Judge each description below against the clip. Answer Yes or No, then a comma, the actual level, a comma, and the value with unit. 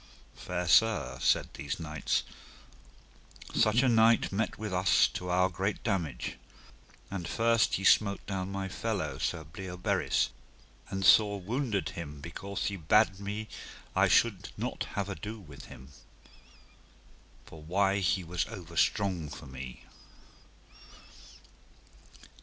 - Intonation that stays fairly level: No, average, 3.8 semitones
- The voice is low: Yes, very low, 95 Hz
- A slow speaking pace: Yes, slow, 125 wpm